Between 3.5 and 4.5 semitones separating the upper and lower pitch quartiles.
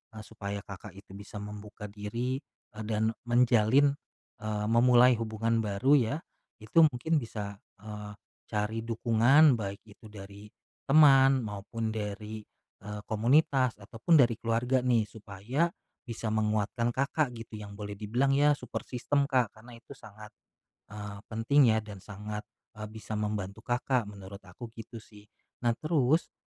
No: average, 3.0 semitones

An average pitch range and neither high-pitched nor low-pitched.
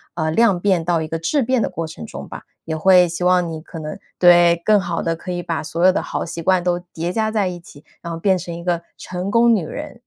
No: narrow, 2.1 semitones; medium, 175 Hz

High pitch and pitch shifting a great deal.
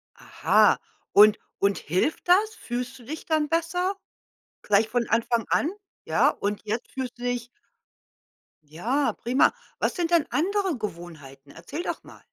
Yes: high, 245 Hz; wide, 7.7 semitones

